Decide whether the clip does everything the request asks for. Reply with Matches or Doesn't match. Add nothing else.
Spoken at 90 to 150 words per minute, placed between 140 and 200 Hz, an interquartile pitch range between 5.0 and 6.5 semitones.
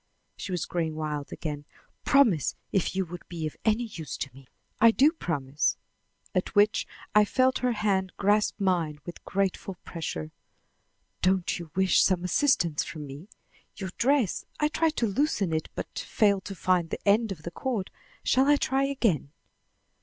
Doesn't match